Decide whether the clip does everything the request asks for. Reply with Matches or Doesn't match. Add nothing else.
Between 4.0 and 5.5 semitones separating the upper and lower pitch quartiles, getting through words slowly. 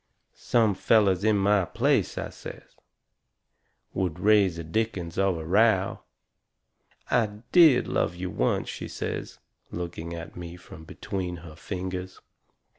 Doesn't match